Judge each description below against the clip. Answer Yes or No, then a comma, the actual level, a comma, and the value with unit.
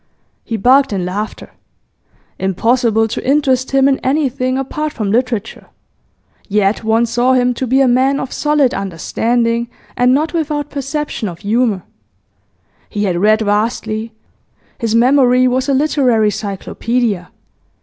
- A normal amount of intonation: Yes, average, 3.7 semitones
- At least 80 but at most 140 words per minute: Yes, slow, 135 wpm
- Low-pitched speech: No, high, 245 Hz